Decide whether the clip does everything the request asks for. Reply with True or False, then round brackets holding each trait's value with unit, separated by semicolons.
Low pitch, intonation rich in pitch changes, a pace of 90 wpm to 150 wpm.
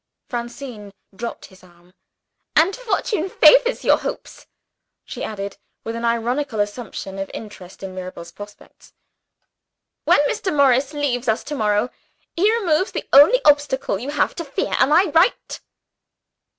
False (255 Hz; 6.7 semitones; 140 wpm)